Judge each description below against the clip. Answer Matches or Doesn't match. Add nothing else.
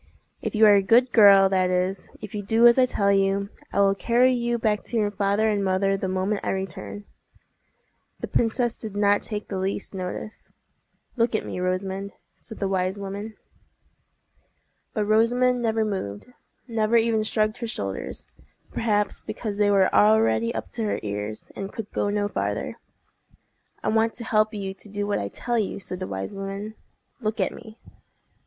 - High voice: Matches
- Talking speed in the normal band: Matches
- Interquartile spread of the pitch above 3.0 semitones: Doesn't match